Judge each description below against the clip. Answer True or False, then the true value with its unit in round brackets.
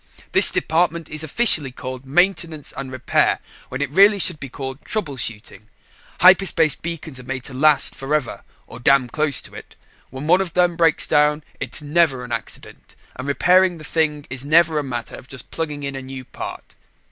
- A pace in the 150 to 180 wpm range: False (190 wpm)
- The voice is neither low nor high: True (150 Hz)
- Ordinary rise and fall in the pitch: True (4.0 semitones)